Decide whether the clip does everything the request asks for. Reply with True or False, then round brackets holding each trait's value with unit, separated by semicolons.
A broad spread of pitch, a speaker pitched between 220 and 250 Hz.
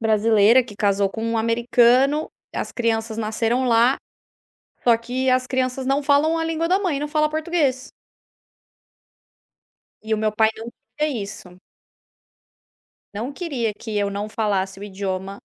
False (4.3 semitones; 230 Hz)